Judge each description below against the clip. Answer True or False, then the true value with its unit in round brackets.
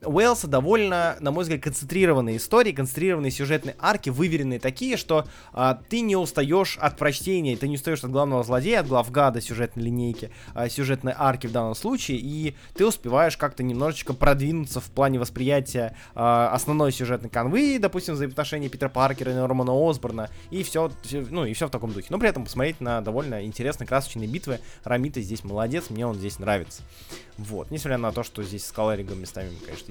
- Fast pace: True (185 wpm)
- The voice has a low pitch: True (130 Hz)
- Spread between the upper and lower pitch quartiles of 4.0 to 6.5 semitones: True (4.4 semitones)